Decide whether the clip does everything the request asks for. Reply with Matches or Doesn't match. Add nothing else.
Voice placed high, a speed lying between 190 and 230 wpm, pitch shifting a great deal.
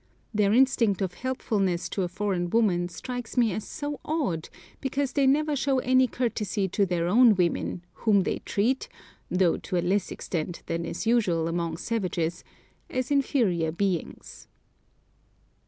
Doesn't match